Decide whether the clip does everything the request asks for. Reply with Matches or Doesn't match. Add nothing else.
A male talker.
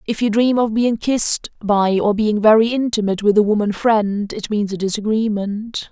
Doesn't match